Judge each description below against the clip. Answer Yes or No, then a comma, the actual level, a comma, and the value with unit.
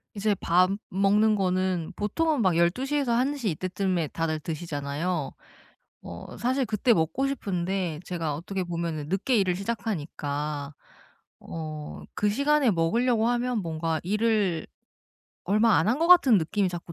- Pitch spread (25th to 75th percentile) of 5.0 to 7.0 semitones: Yes, wide, 5.5 semitones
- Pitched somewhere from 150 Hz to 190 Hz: Yes, medium, 185 Hz